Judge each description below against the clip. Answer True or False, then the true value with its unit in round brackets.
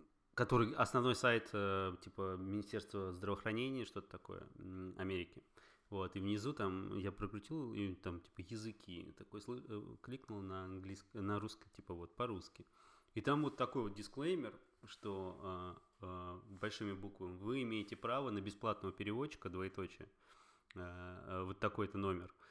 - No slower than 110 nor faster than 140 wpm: True (130 wpm)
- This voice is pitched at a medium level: False (100 Hz)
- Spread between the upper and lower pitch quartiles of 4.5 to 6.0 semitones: False (2.7 semitones)